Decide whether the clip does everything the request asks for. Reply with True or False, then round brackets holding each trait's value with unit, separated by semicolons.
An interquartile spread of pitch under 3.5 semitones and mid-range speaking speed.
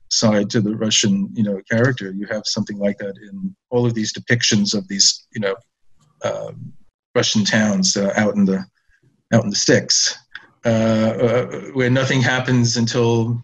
True (2.9 semitones; 170 wpm)